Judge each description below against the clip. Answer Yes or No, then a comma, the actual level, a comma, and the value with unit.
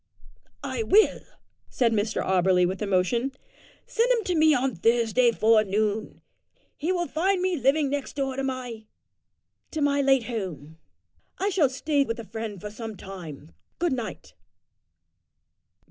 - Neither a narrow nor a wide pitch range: No, wide, 5.7 semitones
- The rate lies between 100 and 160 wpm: Yes, average, 145 wpm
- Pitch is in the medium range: No, high, 240 Hz